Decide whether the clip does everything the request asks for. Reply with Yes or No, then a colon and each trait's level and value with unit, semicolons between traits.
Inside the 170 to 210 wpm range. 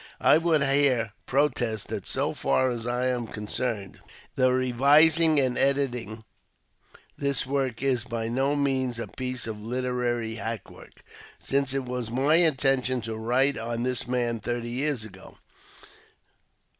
No: average, 145 wpm